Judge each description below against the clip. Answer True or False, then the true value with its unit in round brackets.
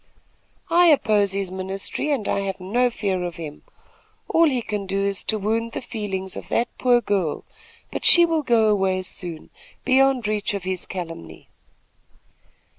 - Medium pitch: False (205 Hz)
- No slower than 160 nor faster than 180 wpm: True (165 wpm)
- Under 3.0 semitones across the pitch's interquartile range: False (4.3 semitones)